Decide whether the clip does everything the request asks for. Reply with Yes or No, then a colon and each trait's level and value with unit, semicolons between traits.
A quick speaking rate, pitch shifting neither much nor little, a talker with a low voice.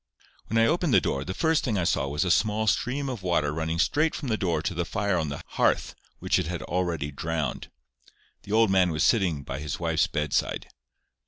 No: fast, 220 wpm; wide, 5.7 semitones; very low, 90 Hz